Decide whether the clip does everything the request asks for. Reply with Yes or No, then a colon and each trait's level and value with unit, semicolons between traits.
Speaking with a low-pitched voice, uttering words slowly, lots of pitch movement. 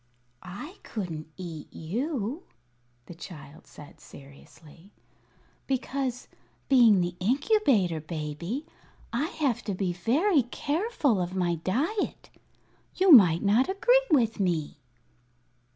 No: high, 210 Hz; slow, 105 wpm; wide, 8.6 semitones